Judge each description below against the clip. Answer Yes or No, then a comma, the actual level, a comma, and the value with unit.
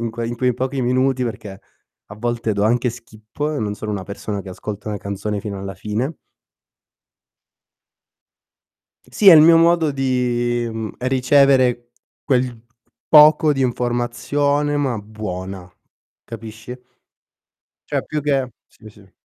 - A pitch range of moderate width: Yes, average, 3.8 semitones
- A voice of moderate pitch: No, low, 120 Hz